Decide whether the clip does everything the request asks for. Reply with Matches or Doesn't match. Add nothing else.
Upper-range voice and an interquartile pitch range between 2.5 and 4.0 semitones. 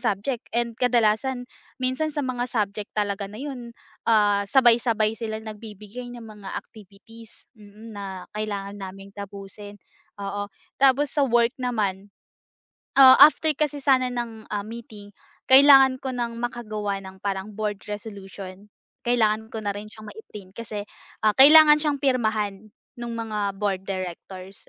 Matches